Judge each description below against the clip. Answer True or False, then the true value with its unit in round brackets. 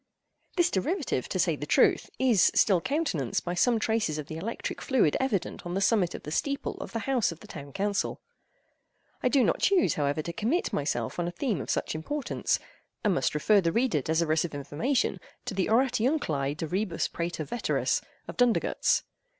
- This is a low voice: False (195 Hz)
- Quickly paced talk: False (190 wpm)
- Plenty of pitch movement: True (7.7 semitones)